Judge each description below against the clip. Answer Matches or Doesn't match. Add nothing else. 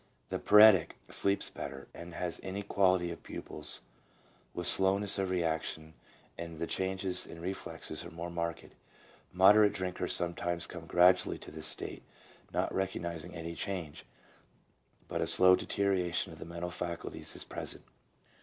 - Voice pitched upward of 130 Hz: Doesn't match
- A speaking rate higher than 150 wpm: Doesn't match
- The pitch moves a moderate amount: Doesn't match